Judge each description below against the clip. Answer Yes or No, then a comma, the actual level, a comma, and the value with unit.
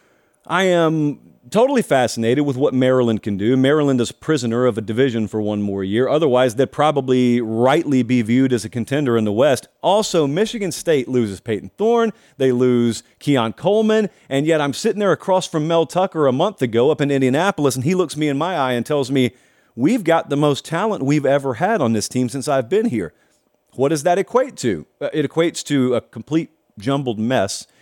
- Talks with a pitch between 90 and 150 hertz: Yes, medium, 140 Hz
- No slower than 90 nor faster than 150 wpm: No, fast, 205 wpm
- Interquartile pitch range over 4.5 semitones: Yes, average, 5.0 semitones